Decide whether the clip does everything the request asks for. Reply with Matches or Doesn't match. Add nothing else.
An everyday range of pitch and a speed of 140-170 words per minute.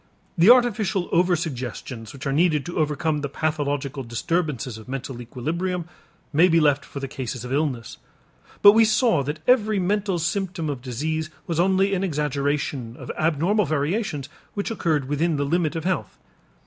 Matches